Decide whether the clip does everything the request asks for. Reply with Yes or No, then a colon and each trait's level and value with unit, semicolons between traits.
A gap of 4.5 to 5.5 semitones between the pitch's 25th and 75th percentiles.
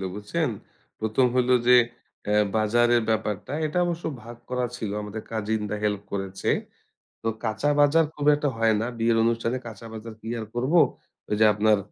No: average, 2.7 semitones